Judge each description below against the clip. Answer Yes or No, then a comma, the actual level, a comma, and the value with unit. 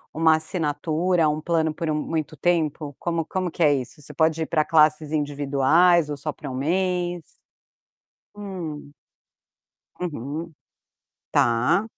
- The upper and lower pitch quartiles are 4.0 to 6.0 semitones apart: No, narrow, 2.5 semitones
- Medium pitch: Yes, medium, 155 Hz